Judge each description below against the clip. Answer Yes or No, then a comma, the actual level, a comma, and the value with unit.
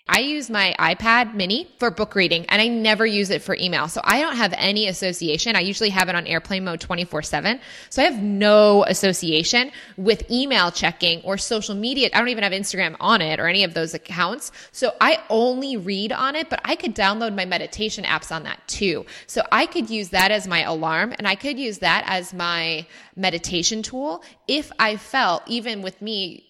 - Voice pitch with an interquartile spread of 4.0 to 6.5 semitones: Yes, average, 4.5 semitones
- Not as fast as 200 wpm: No, fast, 205 wpm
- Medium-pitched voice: No, high, 205 Hz